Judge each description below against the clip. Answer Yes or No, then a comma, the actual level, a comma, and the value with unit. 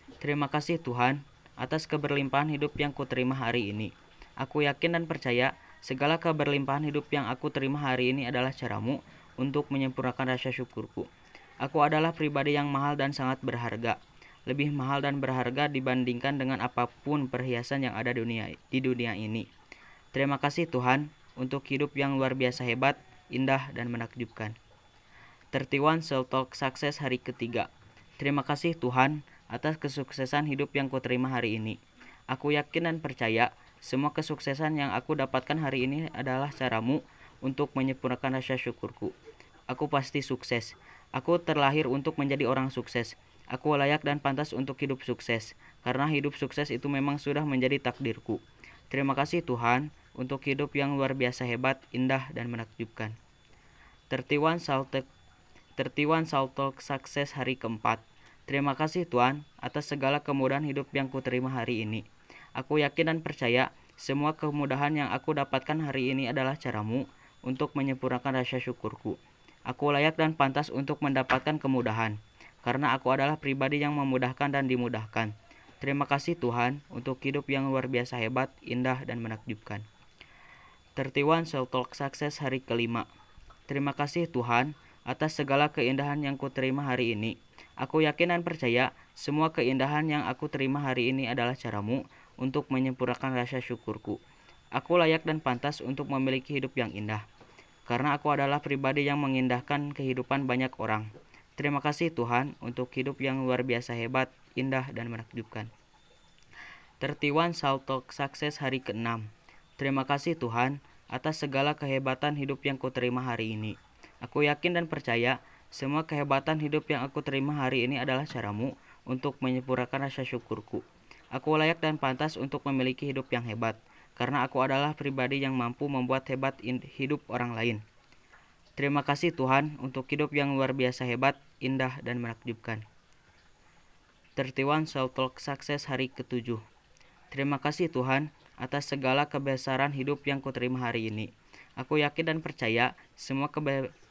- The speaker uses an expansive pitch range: No, narrow, 2.5 semitones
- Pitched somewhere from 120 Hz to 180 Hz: Yes, low, 135 Hz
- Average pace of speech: No, fast, 145 wpm